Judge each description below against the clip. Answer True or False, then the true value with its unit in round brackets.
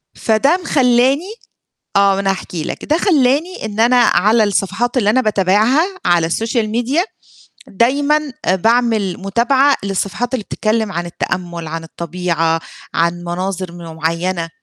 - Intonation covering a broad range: True (6.0 semitones)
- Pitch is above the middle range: True (210 Hz)